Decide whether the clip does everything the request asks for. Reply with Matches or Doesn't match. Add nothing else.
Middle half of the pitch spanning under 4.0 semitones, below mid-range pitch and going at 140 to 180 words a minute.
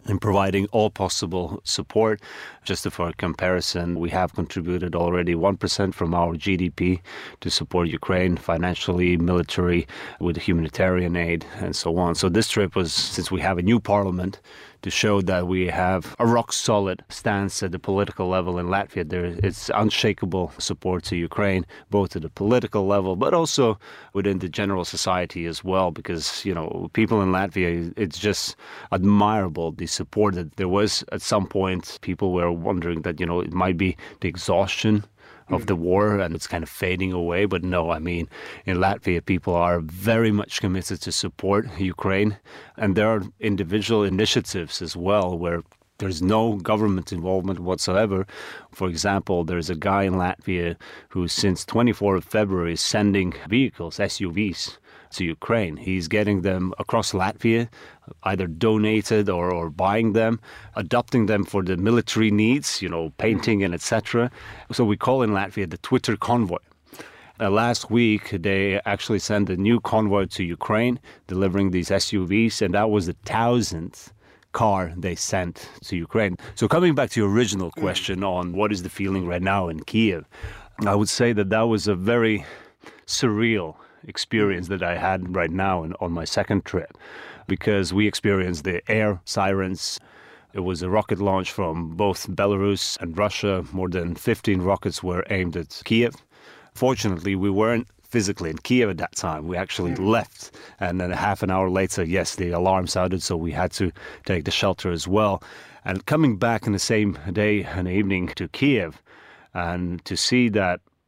Matches